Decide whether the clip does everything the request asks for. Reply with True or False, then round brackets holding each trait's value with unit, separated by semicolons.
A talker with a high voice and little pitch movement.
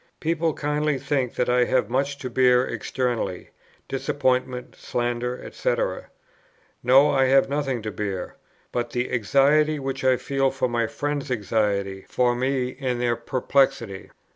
False (130 Hz; 2.3 semitones)